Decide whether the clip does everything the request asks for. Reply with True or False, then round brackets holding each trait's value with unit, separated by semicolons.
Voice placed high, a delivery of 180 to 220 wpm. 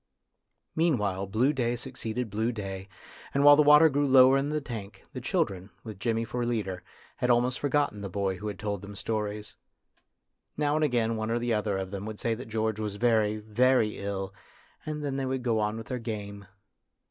False (115 Hz; 195 wpm)